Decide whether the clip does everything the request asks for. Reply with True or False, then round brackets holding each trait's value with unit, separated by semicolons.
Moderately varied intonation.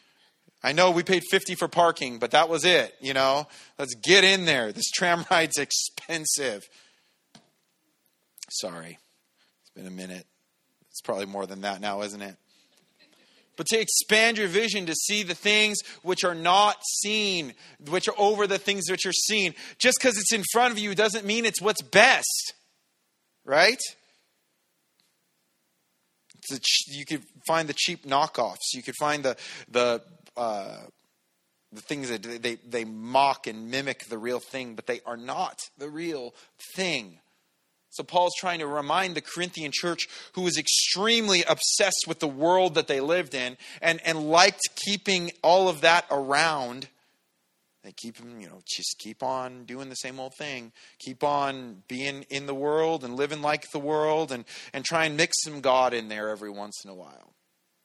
False (6.4 semitones)